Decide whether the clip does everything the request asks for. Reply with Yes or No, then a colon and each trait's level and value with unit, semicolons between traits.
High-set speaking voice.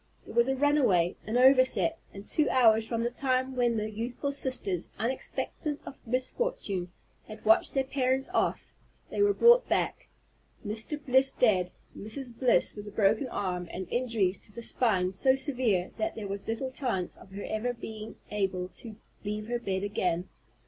Yes: high, 230 Hz